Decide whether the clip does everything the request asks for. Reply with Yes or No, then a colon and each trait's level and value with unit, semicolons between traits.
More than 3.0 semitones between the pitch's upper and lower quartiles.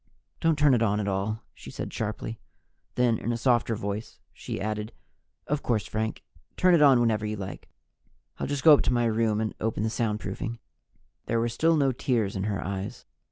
No: average, 2.7 semitones